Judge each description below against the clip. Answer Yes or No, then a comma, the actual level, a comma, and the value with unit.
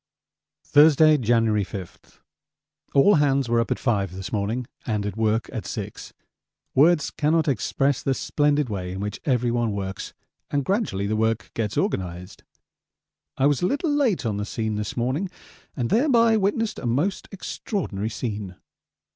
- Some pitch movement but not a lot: No, wide, 6.4 semitones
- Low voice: Yes, low, 120 Hz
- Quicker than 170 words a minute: No, average, 155 wpm